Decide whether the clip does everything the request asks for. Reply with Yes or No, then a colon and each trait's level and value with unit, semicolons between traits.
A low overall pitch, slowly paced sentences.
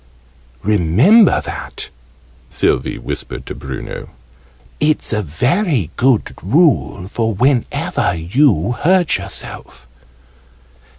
Yes: low, 115 Hz; slow, 85 wpm